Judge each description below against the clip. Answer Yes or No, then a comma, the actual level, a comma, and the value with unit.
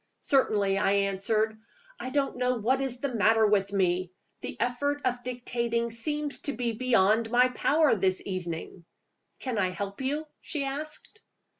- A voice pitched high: Yes, high, 235 Hz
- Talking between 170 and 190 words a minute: No, average, 155 wpm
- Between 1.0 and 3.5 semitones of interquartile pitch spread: No, average, 4.9 semitones